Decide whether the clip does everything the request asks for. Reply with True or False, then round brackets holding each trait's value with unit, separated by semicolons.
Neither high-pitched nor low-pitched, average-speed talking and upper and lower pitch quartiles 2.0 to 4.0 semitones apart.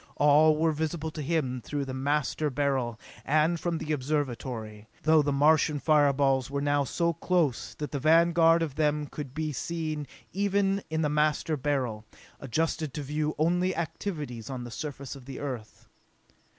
True (150 Hz; 165 wpm; 2.7 semitones)